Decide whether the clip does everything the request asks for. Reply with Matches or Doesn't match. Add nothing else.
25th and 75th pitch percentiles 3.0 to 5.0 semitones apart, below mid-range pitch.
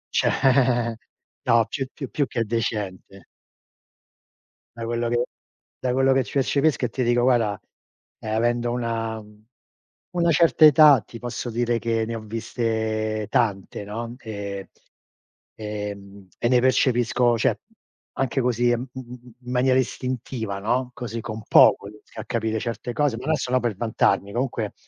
Doesn't match